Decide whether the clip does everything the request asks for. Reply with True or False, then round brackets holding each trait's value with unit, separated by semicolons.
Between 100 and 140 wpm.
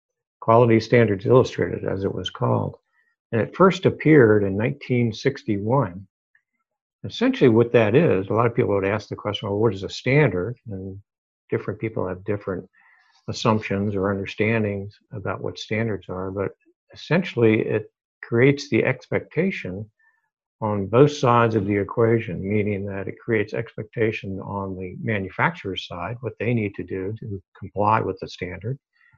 False (150 wpm)